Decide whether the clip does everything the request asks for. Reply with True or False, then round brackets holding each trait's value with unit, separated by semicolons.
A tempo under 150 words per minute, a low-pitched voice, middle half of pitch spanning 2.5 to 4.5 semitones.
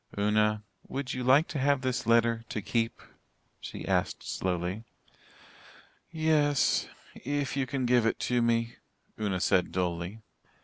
True (135 wpm; 115 Hz; 4.1 semitones)